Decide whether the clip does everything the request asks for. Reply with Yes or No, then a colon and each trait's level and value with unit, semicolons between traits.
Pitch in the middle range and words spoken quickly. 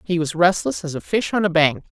Yes: medium, 170 Hz; fast, 270 wpm